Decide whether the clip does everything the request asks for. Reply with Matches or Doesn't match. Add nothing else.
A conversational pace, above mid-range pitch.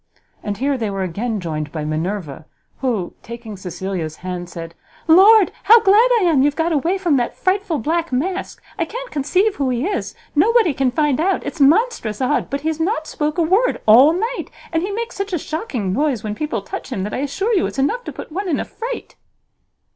Doesn't match